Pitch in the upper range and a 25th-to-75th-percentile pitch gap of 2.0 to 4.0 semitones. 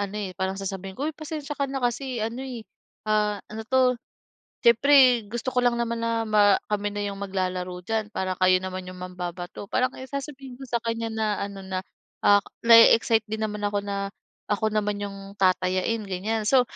Yes: high, 215 Hz; average, 3.5 semitones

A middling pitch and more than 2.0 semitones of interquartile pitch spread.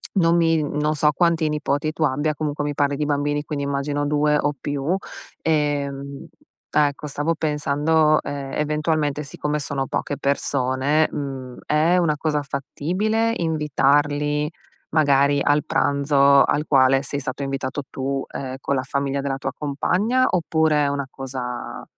No: medium, 145 Hz; narrow, 1.6 semitones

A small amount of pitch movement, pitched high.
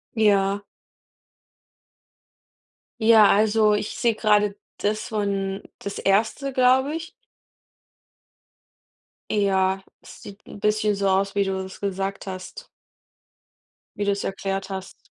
Yes: narrow, 1.9 semitones; high, 200 Hz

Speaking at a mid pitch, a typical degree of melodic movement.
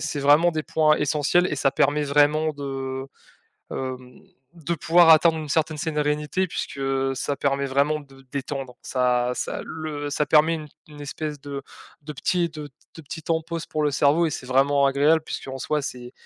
No: medium, 145 Hz; narrow, 2.3 semitones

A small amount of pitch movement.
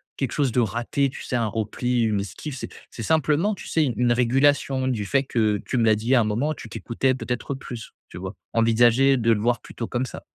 No: average, 3.1 semitones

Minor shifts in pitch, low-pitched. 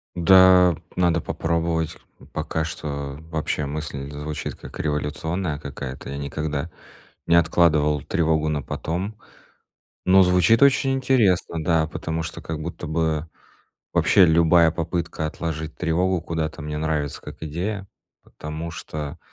Yes: narrow, 2.2 semitones; very low, 80 Hz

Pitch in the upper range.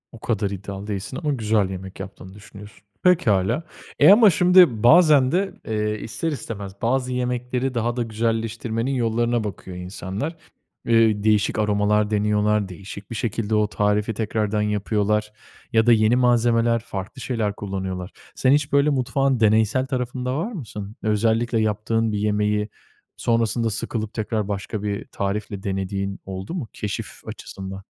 No: low, 110 Hz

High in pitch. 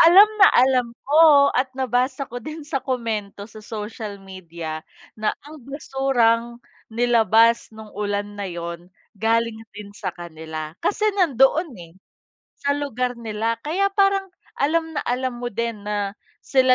Yes: high, 235 Hz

